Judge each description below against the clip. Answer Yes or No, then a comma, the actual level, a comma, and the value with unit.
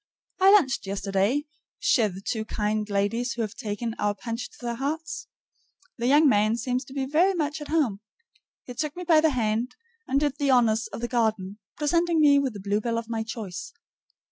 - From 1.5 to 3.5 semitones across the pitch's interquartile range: No, average, 5.2 semitones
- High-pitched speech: Yes, high, 240 Hz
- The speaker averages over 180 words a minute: Yes, average, 195 wpm